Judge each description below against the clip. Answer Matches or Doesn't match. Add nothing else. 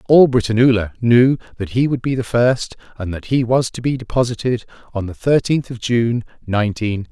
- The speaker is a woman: Doesn't match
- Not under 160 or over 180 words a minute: Doesn't match